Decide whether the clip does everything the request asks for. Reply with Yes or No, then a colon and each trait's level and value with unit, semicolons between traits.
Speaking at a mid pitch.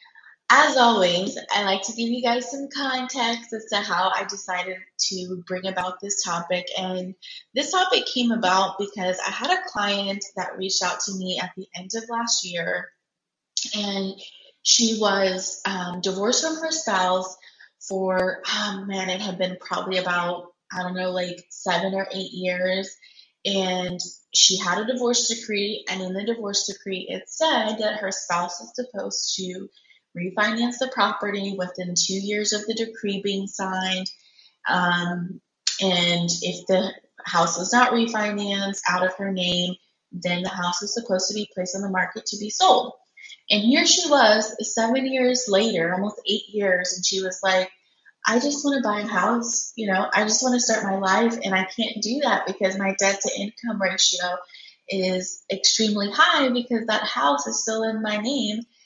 No: high, 195 Hz